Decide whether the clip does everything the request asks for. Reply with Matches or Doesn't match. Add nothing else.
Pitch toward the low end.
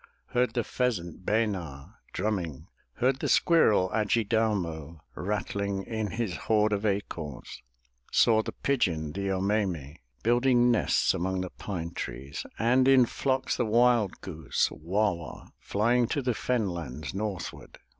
Matches